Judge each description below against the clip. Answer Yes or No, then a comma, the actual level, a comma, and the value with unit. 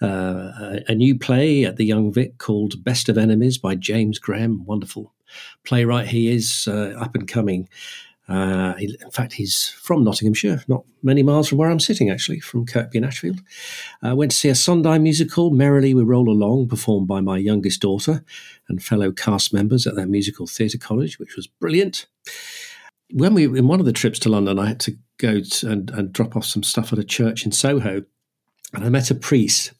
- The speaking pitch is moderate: No, low, 115 Hz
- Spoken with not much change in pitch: No, average, 4.1 semitones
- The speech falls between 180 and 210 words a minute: Yes, fast, 205 wpm